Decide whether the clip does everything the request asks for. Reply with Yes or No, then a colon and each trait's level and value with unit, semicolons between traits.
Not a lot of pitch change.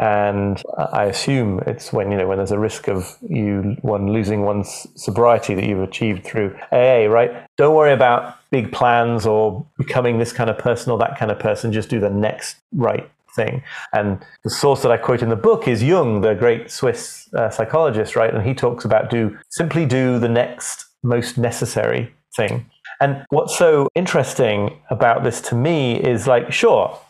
No: average, 3.2 semitones